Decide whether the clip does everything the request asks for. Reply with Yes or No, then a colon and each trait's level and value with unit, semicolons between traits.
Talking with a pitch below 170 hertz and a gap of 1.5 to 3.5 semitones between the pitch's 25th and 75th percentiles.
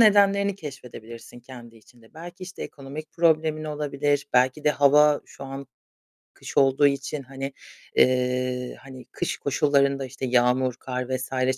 Yes: low, 135 Hz; average, 2.8 semitones